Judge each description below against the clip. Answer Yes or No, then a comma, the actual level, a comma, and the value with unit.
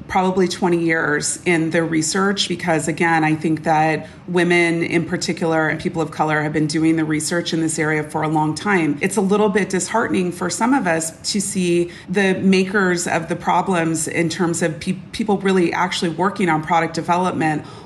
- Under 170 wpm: No, average, 190 wpm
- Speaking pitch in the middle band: Yes, medium, 170 Hz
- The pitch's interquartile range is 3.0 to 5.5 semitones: No, narrow, 2.4 semitones